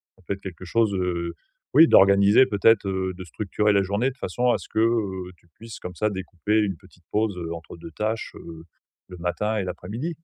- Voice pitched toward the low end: Yes, low, 100 Hz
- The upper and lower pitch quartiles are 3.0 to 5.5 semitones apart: Yes, average, 3.3 semitones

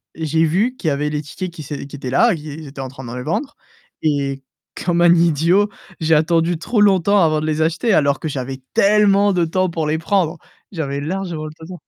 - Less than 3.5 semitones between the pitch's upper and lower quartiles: No, average, 3.8 semitones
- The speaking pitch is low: No, medium, 160 Hz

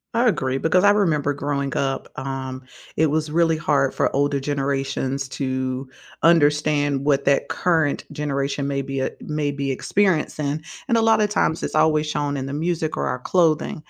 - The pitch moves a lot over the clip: No, narrow, 2.6 semitones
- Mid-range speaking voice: Yes, medium, 145 Hz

